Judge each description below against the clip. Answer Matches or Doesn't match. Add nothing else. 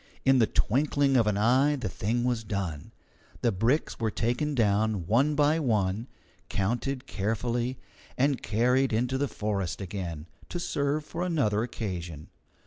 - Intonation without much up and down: Doesn't match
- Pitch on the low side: Matches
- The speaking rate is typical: Matches